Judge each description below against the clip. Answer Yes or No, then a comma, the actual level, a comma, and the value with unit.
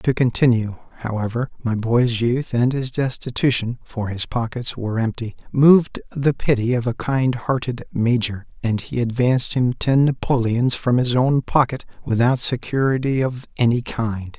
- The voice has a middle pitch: No, low, 120 Hz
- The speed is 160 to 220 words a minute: No, average, 145 wpm